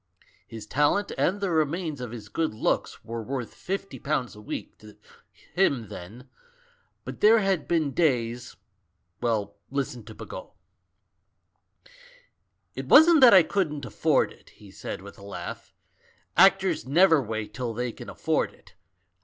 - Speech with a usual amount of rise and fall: No, wide, 7.3 semitones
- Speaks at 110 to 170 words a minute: Yes, average, 150 wpm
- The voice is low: Yes, low, 125 Hz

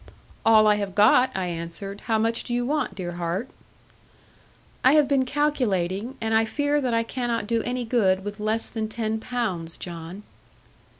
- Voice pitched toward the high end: Yes, high, 220 Hz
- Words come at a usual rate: Yes, average, 175 wpm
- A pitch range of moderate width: Yes, average, 4.3 semitones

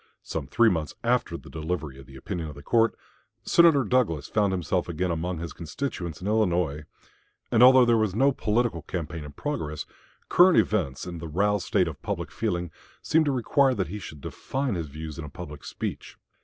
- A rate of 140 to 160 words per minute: No, average, 195 wpm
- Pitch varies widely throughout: Yes, wide, 6.5 semitones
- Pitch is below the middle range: Yes, very low, 90 Hz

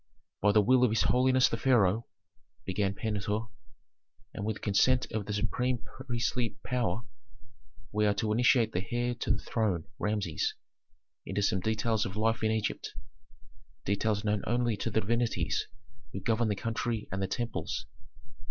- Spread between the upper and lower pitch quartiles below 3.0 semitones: Yes, narrow, 2.5 semitones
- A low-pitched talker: Yes, low, 110 Hz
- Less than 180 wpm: Yes, average, 155 wpm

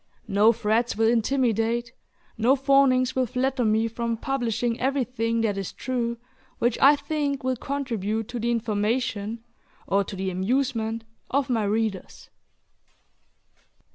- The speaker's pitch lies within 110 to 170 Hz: No, high, 235 Hz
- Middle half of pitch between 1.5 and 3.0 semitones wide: Yes, average, 2.7 semitones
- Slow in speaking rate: Yes, slow, 130 wpm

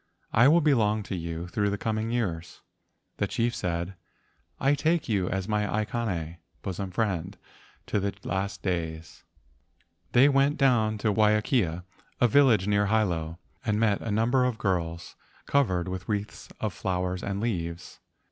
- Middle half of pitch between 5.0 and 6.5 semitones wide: No, average, 4.1 semitones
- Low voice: Yes, low, 105 Hz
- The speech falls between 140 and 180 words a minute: Yes, average, 150 wpm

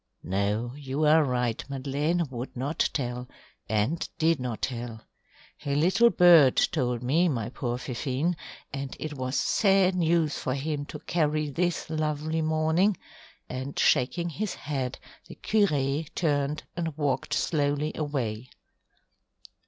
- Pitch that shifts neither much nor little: Yes, average, 4.0 semitones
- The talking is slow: Yes, slow, 130 wpm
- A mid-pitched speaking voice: Yes, medium, 145 Hz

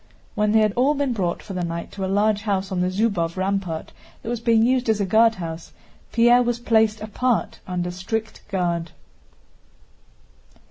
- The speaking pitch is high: Yes, high, 210 Hz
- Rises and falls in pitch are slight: No, average, 3.8 semitones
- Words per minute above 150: Yes, average, 175 wpm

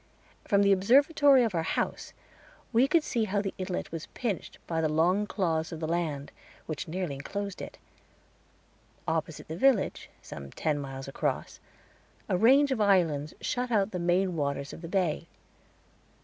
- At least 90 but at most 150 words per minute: No, average, 165 wpm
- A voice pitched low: No, medium, 180 Hz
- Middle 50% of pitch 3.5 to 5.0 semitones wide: Yes, average, 4.7 semitones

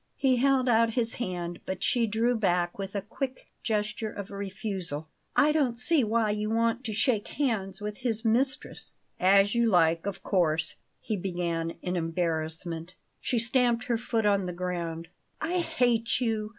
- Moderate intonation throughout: Yes, average, 4.7 semitones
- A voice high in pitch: Yes, high, 210 Hz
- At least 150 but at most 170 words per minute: Yes, average, 165 wpm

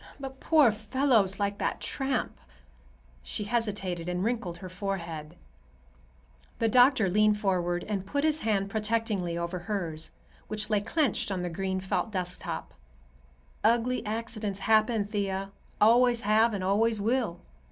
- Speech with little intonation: No, average, 3.4 semitones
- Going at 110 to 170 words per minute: Yes, slow, 135 wpm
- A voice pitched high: Yes, high, 210 Hz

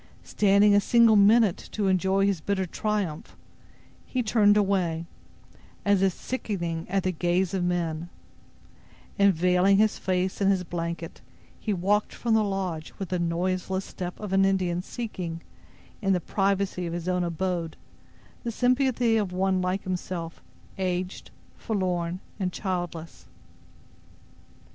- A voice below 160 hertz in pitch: No, high, 190 Hz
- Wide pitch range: No, narrow, 2.4 semitones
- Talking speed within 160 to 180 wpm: No, average, 140 wpm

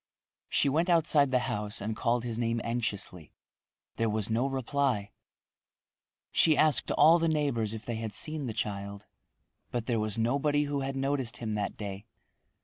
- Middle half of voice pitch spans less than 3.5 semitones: No, average, 4.7 semitones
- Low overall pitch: Yes, low, 120 Hz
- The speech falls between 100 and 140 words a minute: No, average, 165 wpm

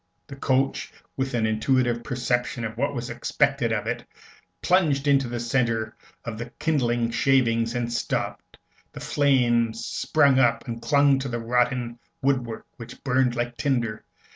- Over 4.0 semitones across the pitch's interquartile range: No, narrow, 2.4 semitones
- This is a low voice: Yes, low, 120 Hz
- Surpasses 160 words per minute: No, average, 150 wpm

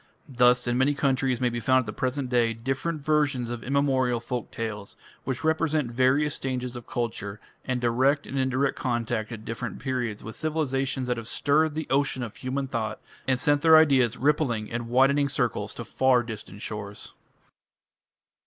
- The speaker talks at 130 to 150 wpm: No, average, 170 wpm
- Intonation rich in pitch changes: No, average, 2.9 semitones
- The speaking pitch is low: Yes, low, 130 Hz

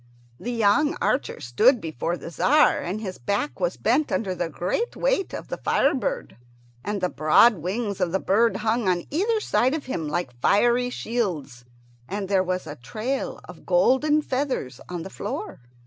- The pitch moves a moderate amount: No, wide, 6.6 semitones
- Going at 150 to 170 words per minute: No, average, 180 wpm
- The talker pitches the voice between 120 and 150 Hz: No, high, 205 Hz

